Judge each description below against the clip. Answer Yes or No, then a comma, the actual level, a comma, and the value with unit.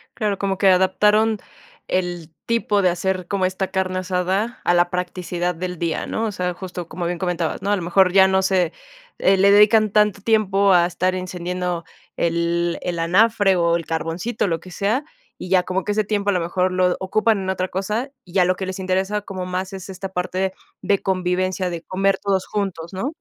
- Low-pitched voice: No, medium, 185 Hz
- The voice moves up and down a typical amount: No, narrow, 1.9 semitones